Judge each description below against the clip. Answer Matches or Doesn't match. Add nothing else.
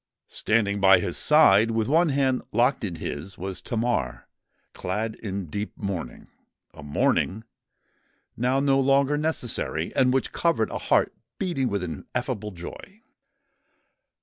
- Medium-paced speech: Doesn't match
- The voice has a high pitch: Doesn't match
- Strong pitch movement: Matches